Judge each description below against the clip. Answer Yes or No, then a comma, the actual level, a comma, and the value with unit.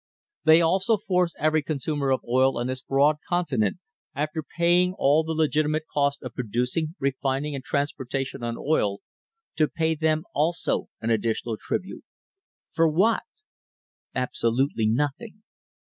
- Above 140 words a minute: No, slow, 135 wpm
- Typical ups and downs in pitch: Yes, average, 3.7 semitones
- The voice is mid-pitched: Yes, medium, 145 Hz